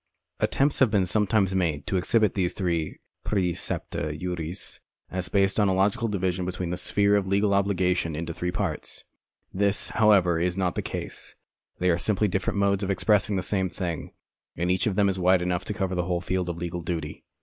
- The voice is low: Yes, very low, 95 Hz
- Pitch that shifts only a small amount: Yes, narrow, 2.1 semitones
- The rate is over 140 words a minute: Yes, average, 195 wpm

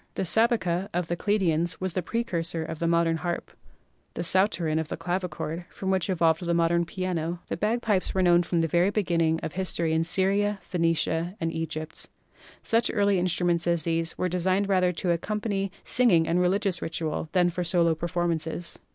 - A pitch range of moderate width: No, narrow, 2.3 semitones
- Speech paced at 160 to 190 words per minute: Yes, average, 175 wpm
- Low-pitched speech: No, medium, 175 Hz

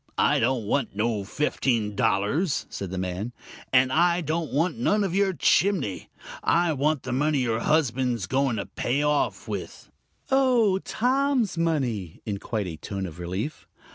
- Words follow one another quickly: No, average, 165 wpm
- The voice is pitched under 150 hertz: Yes, low, 135 Hz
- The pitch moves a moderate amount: No, wide, 8.0 semitones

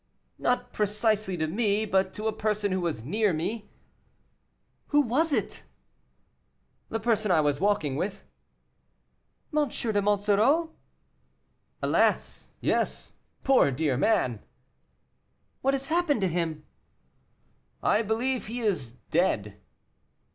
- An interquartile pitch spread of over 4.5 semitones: Yes, wide, 5.4 semitones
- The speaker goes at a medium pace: No, slow, 115 wpm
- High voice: Yes, high, 210 Hz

